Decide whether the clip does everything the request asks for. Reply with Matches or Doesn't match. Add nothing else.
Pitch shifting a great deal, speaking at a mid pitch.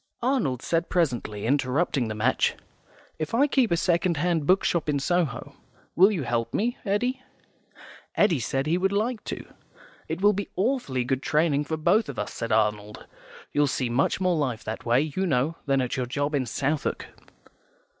Matches